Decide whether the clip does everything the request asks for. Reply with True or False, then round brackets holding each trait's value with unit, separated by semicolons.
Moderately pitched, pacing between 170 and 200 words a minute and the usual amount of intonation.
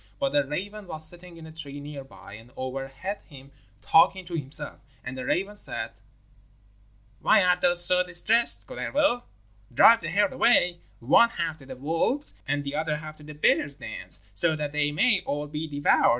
True (155 Hz; 185 wpm; 4.1 semitones)